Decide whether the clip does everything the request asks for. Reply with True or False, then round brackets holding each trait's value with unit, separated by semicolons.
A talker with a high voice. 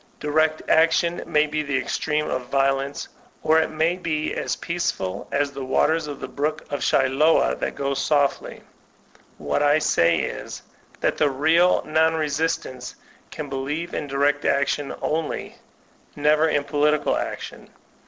False (150 Hz)